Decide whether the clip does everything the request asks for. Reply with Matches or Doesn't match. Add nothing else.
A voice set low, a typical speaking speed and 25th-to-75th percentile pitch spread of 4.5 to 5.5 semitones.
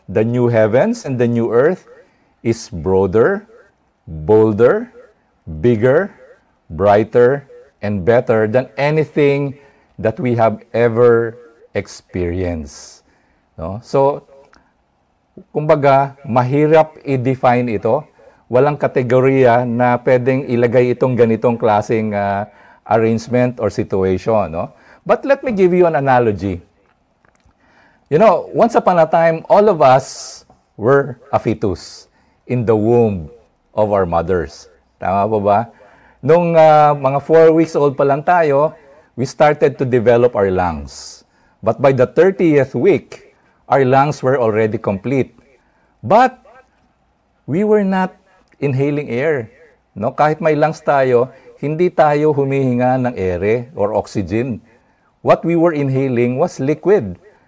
Doesn't match